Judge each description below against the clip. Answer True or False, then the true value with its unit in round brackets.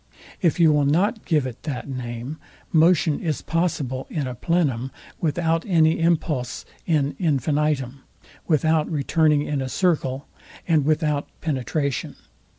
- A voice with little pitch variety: False (3.4 semitones)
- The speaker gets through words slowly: True (130 wpm)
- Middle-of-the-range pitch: True (150 Hz)